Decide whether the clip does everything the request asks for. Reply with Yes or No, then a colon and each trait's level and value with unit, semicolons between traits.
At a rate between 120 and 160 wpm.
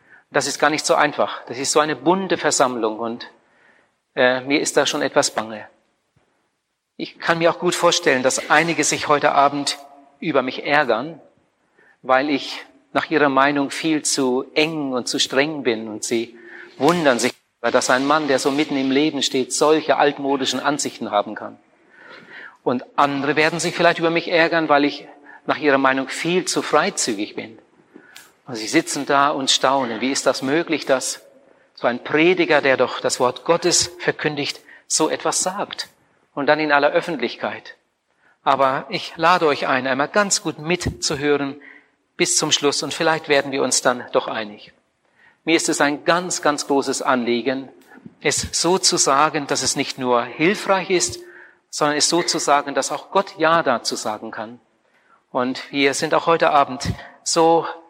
No: average, 170 wpm